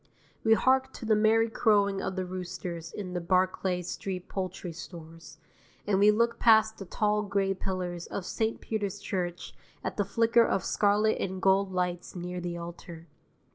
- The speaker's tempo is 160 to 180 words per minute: Yes, average, 170 wpm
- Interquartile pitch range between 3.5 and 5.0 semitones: No, average, 3.0 semitones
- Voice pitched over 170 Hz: Yes, high, 190 Hz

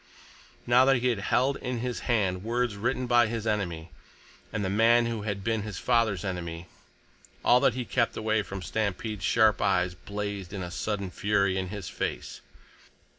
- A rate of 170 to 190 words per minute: Yes, average, 175 wpm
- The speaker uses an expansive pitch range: No, average, 3.4 semitones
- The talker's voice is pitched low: Yes, low, 105 Hz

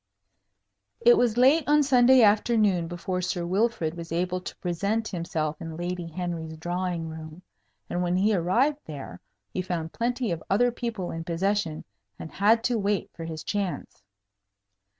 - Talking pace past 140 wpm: Yes, average, 155 wpm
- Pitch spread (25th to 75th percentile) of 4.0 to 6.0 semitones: Yes, average, 5.0 semitones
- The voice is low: No, medium, 180 Hz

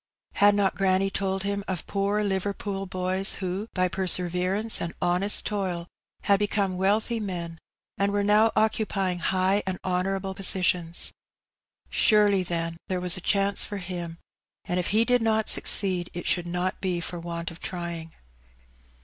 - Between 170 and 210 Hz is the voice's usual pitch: Yes, high, 190 Hz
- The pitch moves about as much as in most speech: No, narrow, 2.2 semitones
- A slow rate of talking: No, average, 155 wpm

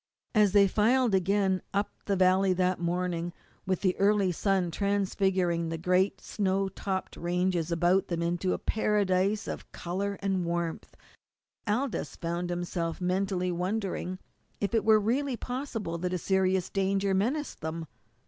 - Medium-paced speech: Yes, average, 145 wpm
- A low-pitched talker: No, high, 190 Hz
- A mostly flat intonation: Yes, narrow, 2.3 semitones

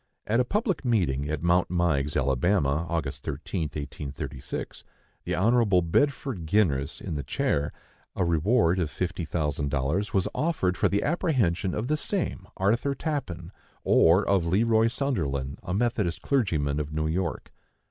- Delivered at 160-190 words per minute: No, average, 150 wpm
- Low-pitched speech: Yes, very low, 90 Hz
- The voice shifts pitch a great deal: Yes, wide, 7.2 semitones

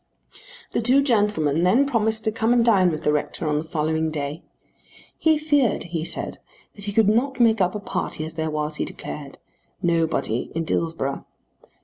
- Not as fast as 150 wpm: No, average, 185 wpm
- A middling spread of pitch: No, wide, 6.3 semitones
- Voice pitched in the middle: Yes, medium, 180 Hz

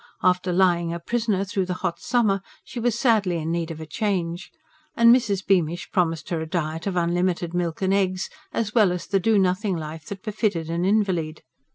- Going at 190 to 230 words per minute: Yes, average, 200 wpm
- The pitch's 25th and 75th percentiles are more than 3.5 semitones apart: No, average, 3.1 semitones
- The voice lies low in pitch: No, medium, 185 Hz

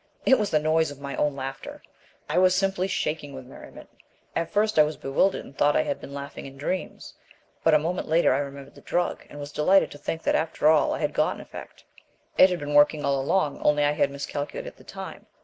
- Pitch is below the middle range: No, medium, 150 Hz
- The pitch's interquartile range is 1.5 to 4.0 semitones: Yes, average, 3.7 semitones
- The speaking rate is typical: No, fast, 235 wpm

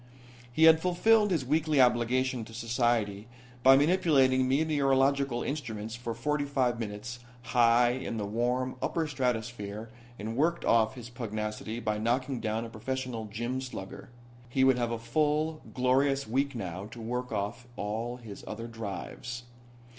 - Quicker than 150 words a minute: No, average, 145 wpm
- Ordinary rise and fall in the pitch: Yes, average, 3.2 semitones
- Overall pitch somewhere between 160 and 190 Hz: No, low, 120 Hz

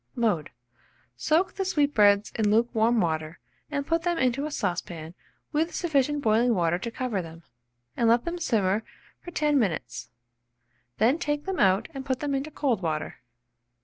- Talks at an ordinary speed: Yes, average, 160 wpm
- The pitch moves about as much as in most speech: No, wide, 7.0 semitones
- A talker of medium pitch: No, high, 240 Hz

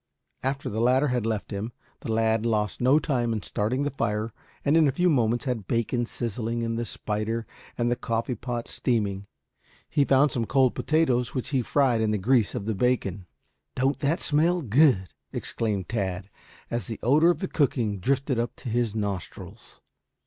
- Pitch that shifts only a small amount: No, average, 3.5 semitones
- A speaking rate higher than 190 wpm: No, average, 185 wpm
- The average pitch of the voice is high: No, low, 120 Hz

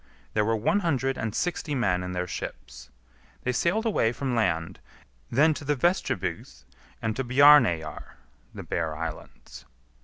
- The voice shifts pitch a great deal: Yes, wide, 8.2 semitones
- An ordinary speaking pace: Yes, average, 150 wpm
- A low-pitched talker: Yes, low, 115 Hz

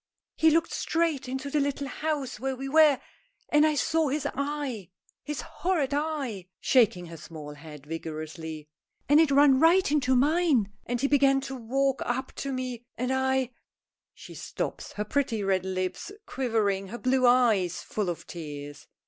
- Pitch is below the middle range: No, very high, 260 Hz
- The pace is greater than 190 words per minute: No, average, 165 wpm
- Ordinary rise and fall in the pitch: No, wide, 6.5 semitones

